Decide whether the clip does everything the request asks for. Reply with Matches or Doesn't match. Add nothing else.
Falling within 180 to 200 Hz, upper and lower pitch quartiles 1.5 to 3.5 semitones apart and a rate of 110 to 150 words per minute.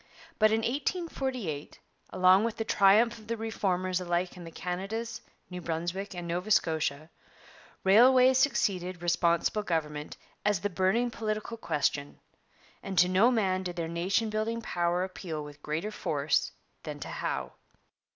Doesn't match